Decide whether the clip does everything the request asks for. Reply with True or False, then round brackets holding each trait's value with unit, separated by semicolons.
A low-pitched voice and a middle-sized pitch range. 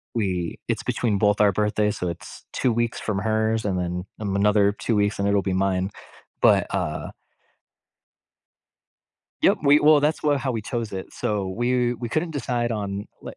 True (105 Hz; 3.3 semitones)